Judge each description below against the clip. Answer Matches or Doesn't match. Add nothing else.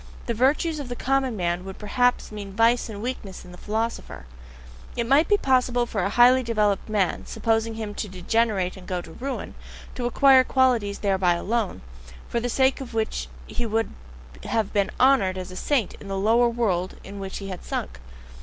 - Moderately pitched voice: Doesn't match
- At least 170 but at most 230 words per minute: Matches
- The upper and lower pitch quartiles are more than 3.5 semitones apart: Matches